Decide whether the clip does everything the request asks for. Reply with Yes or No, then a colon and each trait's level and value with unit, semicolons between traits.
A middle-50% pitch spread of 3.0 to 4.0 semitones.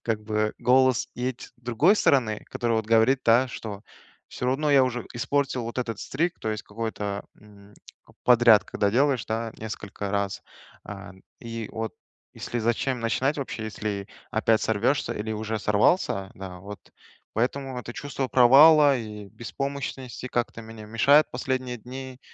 Yes: average, 3.3 semitones